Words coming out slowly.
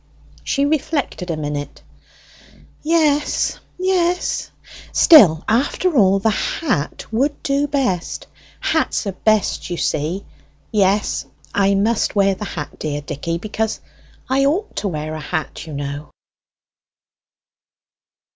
Yes: slow, 120 wpm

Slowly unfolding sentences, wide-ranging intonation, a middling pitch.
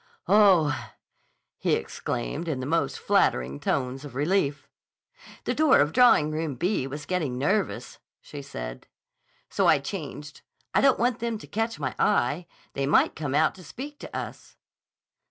No: average, 155 wpm; wide, 6.4 semitones; medium, 150 Hz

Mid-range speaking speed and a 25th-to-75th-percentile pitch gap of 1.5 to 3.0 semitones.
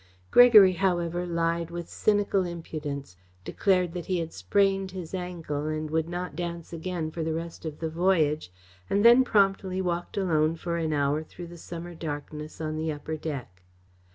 Yes: average, 170 wpm; average, 2.7 semitones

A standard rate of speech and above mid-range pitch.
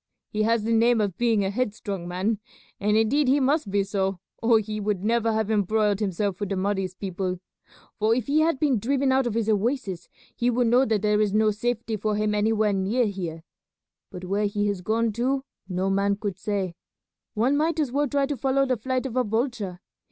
No: fast, 210 wpm; high, 215 Hz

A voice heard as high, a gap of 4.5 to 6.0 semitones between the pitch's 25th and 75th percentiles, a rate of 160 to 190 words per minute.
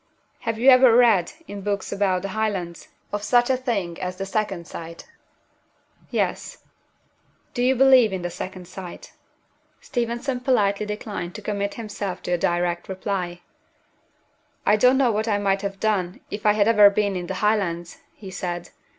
No: high, 200 Hz; average, 3.4 semitones; average, 170 wpm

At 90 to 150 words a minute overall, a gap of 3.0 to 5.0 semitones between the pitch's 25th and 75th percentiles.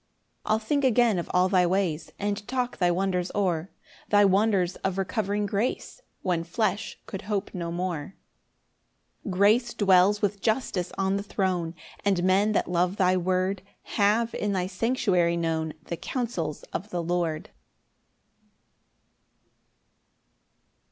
No: average, 140 wpm; narrow, 2.6 semitones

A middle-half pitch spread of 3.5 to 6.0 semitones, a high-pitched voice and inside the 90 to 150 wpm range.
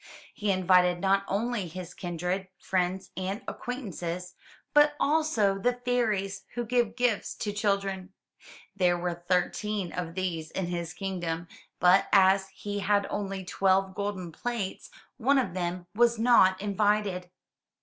No: average, 2.7 semitones; high, 195 Hz; slow, 135 wpm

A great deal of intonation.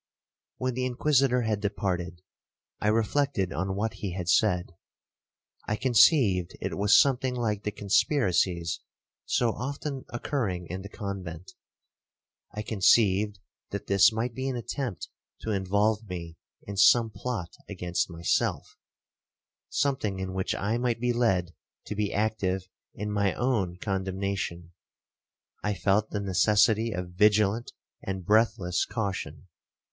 No: average, 3.5 semitones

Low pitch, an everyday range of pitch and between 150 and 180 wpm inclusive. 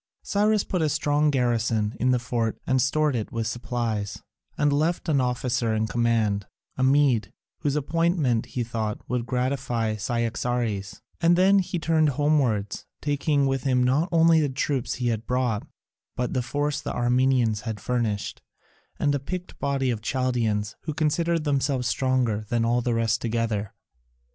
Yes: low, 125 Hz; average, 4.0 semitones; average, 160 wpm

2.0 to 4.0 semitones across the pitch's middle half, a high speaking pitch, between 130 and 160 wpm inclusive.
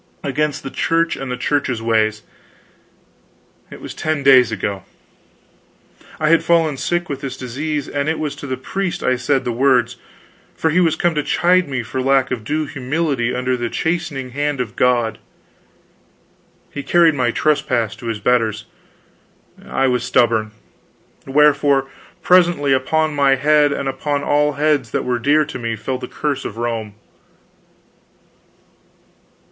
No: average, 3.4 semitones; low, 135 Hz; average, 155 wpm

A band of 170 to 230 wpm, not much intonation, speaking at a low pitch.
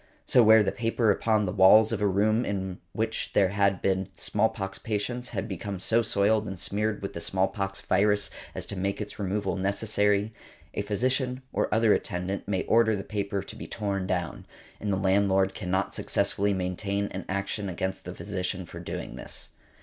Yes: average, 180 wpm; narrow, 2.0 semitones; low, 100 Hz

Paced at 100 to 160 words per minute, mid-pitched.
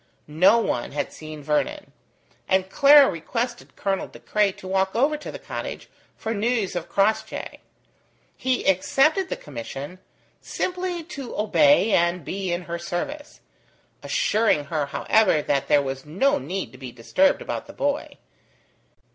No: average, 145 wpm; high, 195 Hz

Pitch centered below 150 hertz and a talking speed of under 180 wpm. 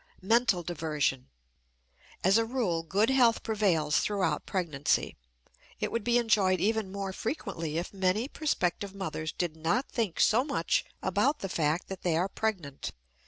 No: high, 190 Hz; average, 150 wpm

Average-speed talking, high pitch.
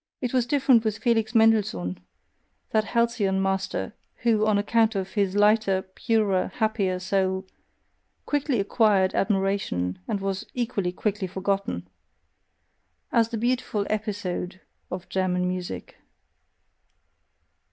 No: slow, 110 wpm; high, 200 Hz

